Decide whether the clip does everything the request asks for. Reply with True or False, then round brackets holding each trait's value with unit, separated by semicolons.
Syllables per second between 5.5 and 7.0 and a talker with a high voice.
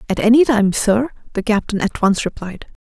False (5.2 syllables/s; 220 Hz)